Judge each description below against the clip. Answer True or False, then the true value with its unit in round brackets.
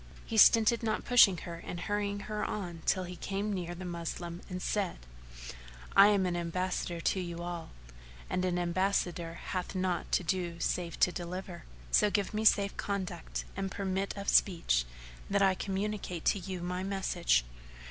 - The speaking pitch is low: False (185 Hz)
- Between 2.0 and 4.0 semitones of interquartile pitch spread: True (2.4 semitones)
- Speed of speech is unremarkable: True (170 wpm)